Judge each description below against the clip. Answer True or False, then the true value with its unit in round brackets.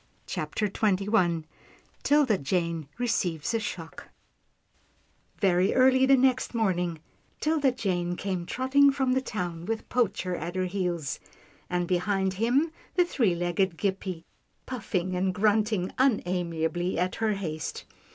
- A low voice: False (190 Hz)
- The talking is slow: True (125 wpm)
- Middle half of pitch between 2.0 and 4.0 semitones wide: False (4.9 semitones)